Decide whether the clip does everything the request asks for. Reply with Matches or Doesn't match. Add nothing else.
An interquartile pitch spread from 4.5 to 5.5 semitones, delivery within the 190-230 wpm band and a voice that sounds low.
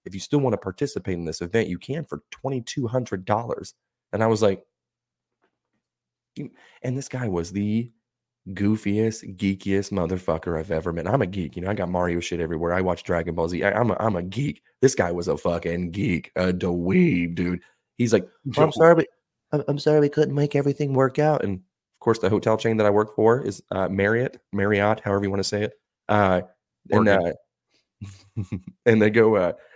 Matches